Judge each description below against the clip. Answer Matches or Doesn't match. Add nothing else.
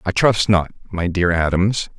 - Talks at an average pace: Matches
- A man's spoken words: Matches